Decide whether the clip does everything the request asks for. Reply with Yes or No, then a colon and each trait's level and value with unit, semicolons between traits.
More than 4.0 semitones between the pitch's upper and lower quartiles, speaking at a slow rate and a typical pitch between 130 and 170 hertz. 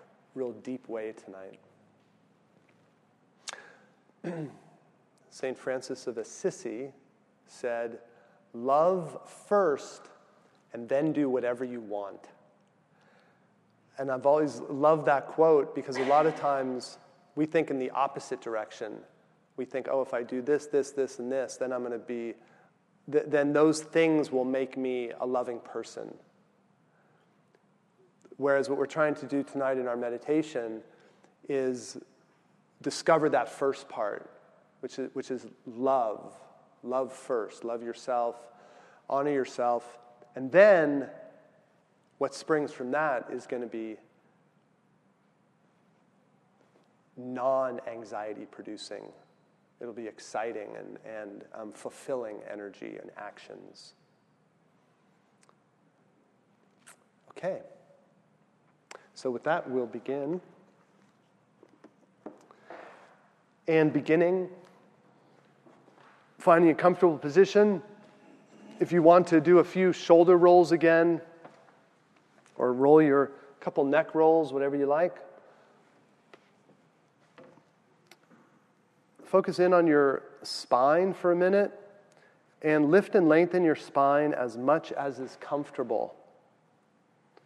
Yes: average, 4.7 semitones; slow, 110 wpm; medium, 140 Hz